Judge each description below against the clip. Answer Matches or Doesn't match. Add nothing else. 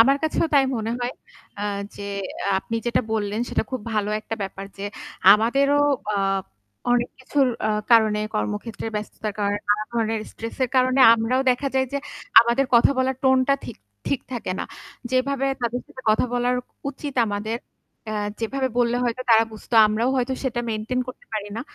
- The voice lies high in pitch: Matches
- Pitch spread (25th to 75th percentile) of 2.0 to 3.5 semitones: Matches